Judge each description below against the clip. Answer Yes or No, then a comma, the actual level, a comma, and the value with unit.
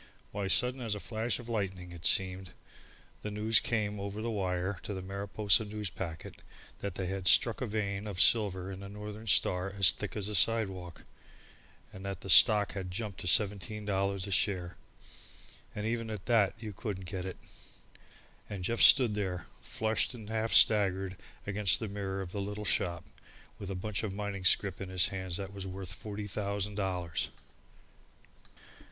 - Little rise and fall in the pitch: Yes, narrow, 2.0 semitones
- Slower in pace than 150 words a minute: No, average, 175 wpm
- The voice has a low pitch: Yes, low, 100 Hz